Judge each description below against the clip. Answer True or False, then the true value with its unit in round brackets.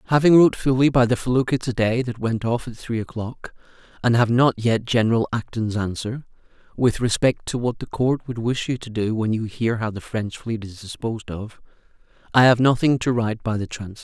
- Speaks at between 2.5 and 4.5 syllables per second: False (5.5 syllables/s)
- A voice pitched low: True (115 Hz)